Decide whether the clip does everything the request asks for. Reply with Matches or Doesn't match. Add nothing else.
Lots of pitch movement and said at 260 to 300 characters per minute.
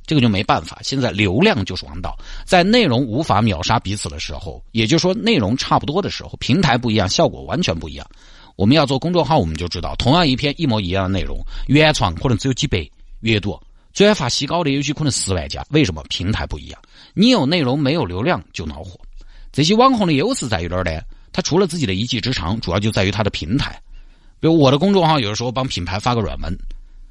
Doesn't match